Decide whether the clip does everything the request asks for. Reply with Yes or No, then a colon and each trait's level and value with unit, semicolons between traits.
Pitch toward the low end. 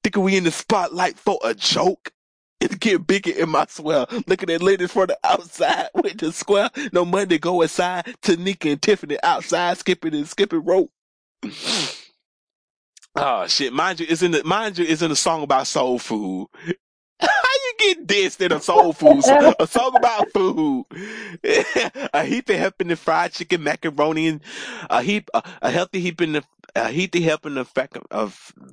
No: medium, 180 Hz